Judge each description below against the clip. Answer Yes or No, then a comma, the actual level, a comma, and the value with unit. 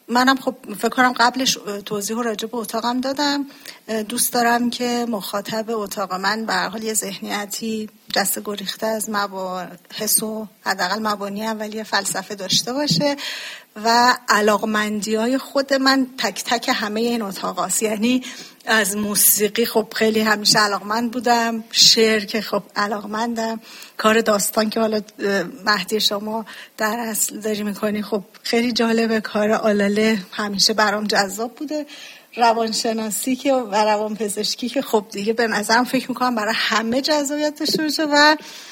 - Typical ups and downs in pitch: No, narrow, 2.3 semitones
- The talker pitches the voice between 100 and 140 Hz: No, high, 220 Hz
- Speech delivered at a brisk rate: No, average, 140 wpm